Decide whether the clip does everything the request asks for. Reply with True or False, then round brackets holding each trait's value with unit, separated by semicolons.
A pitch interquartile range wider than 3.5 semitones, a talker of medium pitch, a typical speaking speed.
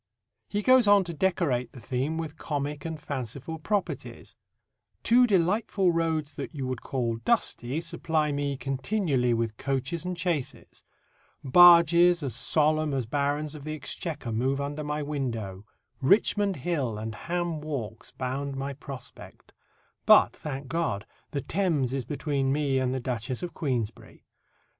True (4.4 semitones; 145 Hz; 145 wpm)